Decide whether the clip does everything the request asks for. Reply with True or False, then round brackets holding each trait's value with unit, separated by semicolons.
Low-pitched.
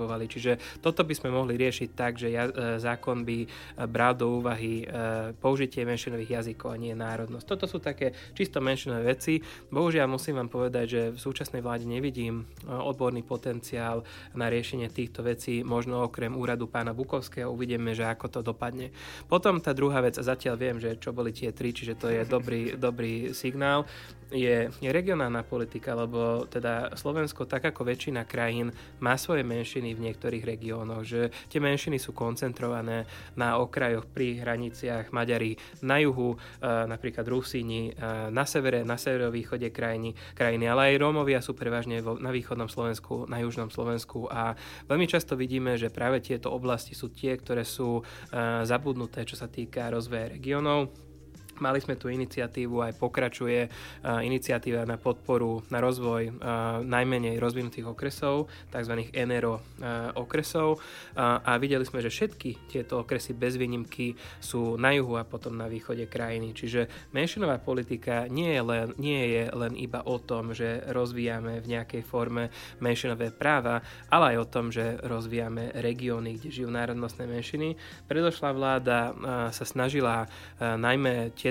True (120 Hz)